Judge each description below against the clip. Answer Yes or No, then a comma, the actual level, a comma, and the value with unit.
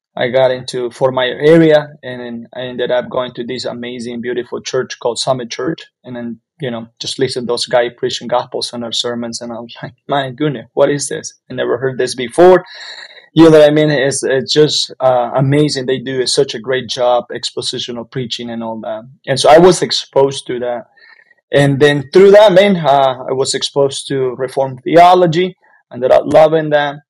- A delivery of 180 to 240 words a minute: Yes, fast, 205 wpm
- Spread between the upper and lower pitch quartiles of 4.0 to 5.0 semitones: No, average, 3.3 semitones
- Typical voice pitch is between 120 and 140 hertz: Yes, low, 130 Hz